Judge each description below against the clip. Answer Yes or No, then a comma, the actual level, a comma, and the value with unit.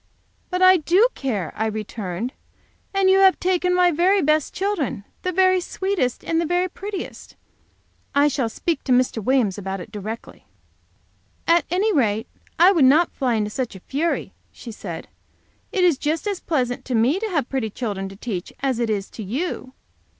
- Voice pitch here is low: No, very high, 275 Hz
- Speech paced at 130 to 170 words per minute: No, average, 180 wpm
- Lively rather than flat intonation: Yes, wide, 8.4 semitones